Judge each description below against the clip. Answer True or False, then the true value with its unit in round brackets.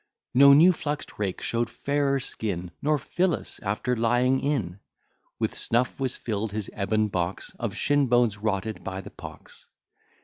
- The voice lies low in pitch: True (115 Hz)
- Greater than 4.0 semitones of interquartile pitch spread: True (5.3 semitones)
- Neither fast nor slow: True (150 wpm)